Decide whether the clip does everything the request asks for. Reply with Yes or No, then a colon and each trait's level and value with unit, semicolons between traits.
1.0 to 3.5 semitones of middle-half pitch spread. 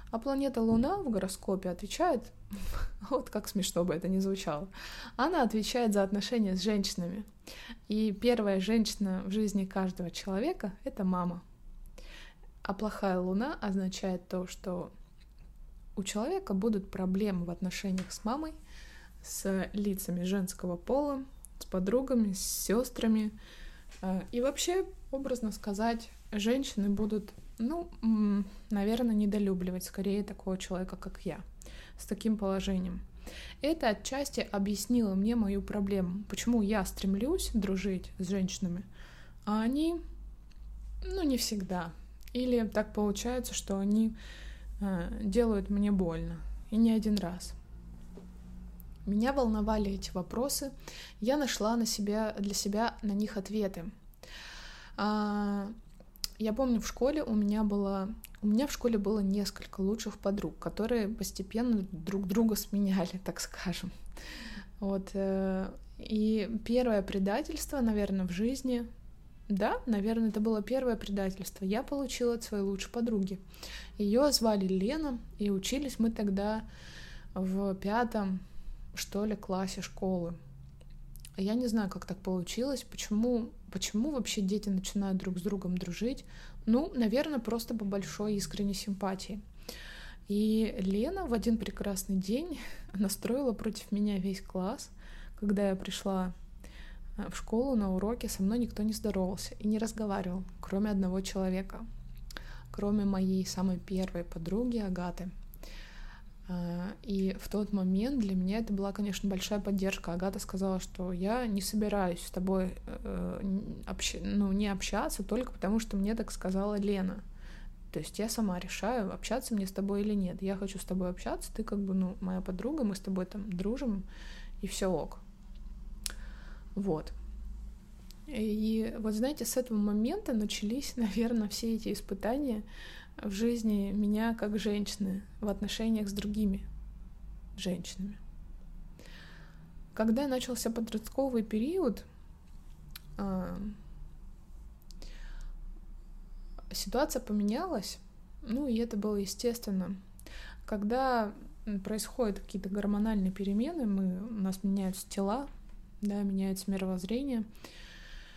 Yes: average, 2.9 semitones